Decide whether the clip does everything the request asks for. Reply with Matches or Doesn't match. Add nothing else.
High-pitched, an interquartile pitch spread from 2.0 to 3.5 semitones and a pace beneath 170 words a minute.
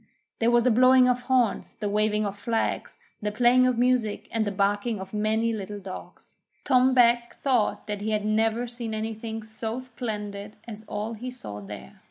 Doesn't match